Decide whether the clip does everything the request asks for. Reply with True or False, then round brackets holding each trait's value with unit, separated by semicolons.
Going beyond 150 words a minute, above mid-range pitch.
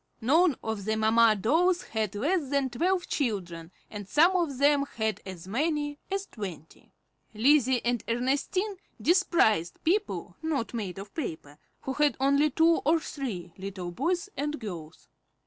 False (145 wpm; 260 Hz)